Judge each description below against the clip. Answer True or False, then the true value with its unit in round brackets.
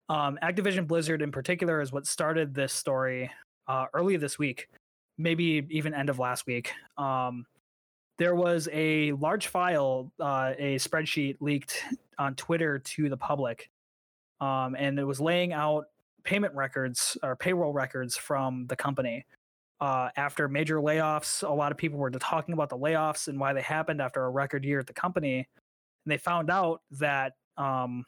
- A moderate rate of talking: True (170 wpm)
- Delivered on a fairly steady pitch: False (3.2 semitones)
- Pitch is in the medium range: True (145 Hz)